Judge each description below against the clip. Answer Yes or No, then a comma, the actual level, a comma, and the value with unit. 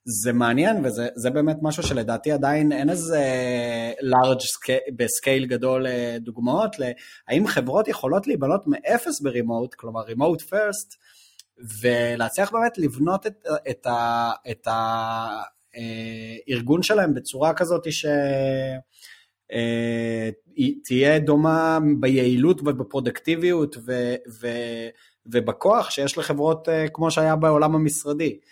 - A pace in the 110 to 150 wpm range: No, slow, 100 wpm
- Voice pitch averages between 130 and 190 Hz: Yes, low, 135 Hz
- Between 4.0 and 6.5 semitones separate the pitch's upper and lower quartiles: Yes, average, 4.8 semitones